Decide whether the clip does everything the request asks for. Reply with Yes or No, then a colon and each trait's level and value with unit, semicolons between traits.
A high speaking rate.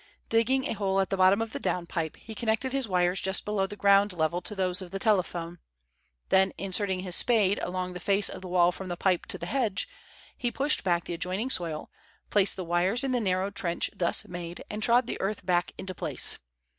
Yes: fast, 220 wpm